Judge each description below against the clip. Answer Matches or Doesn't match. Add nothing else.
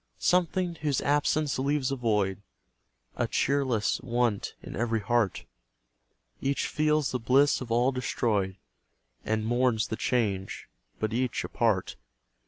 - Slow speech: Matches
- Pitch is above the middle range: Doesn't match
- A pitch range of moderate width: Matches